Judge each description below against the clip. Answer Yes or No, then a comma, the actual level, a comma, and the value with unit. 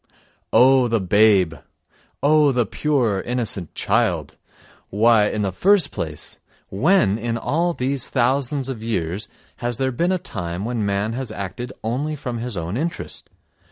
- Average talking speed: Yes, average, 150 wpm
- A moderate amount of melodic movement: Yes, average, 4.7 semitones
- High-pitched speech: No, low, 120 Hz